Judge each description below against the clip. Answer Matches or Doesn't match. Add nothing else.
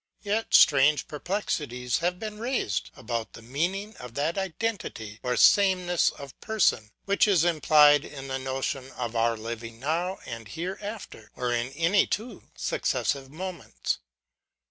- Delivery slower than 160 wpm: Matches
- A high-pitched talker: Doesn't match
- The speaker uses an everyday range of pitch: Doesn't match